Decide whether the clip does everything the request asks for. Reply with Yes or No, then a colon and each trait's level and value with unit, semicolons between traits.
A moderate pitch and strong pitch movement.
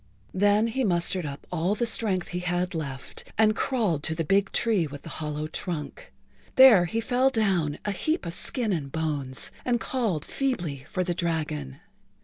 Yes: medium, 180 Hz; wide, 6.0 semitones